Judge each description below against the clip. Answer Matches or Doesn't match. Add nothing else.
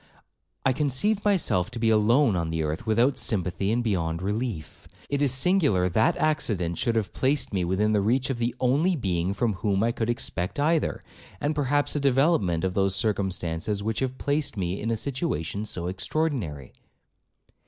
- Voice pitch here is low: Matches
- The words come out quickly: Doesn't match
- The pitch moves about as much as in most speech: Doesn't match